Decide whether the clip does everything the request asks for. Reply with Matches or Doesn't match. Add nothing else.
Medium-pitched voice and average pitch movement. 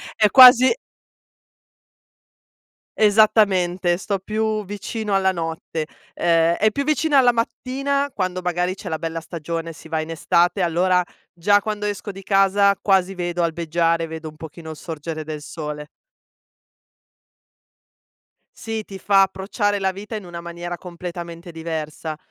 Matches